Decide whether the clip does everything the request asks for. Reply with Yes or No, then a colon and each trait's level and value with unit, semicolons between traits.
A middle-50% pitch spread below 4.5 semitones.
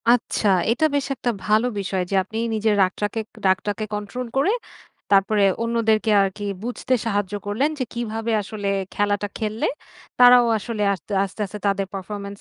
Yes: narrow, 2.6 semitones